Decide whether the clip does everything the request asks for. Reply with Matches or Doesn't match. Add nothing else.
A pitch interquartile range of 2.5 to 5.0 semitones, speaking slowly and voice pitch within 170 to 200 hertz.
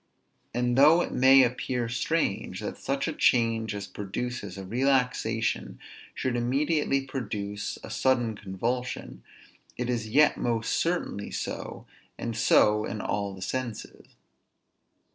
Doesn't match